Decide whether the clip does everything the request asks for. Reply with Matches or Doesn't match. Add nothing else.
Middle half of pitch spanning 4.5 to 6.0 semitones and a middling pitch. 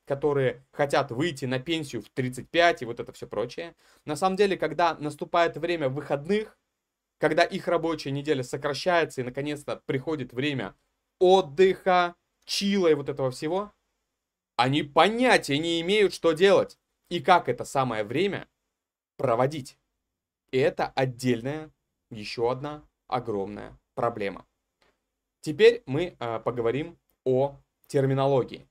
Matches